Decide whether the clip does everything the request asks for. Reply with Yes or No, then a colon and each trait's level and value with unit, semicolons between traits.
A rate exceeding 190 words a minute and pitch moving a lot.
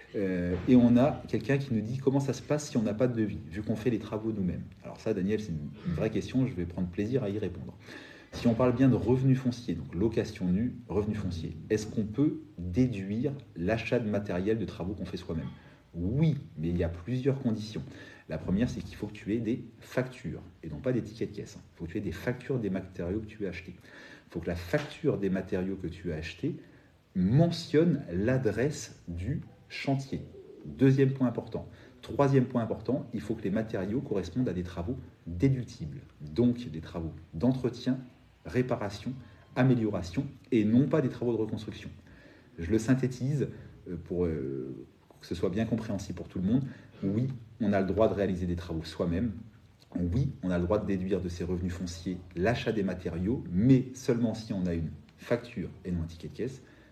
Yes: average, 205 wpm; wide, 5.7 semitones